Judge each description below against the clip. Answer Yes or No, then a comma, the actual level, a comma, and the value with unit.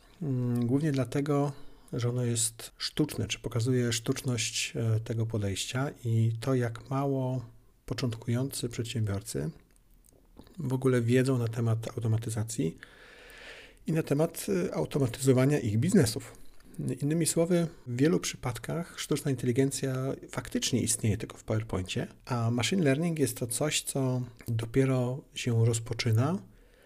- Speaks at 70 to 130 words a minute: Yes, average, 115 wpm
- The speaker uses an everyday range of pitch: Yes, average, 3.2 semitones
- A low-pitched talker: Yes, low, 125 Hz